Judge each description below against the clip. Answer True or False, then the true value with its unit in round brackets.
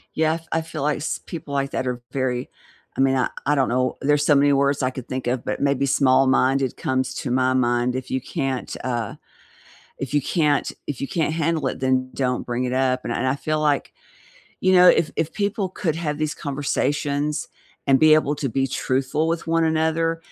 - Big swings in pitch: False (3.1 semitones)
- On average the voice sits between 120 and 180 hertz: True (140 Hz)